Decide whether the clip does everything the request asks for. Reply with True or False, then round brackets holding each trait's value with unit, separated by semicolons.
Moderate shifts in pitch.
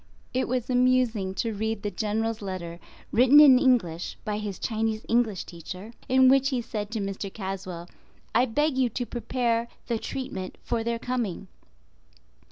True (4.1 semitones)